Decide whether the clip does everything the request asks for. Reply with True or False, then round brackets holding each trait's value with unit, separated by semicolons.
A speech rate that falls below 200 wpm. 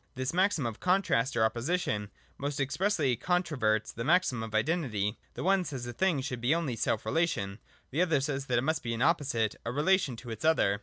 False (205 wpm)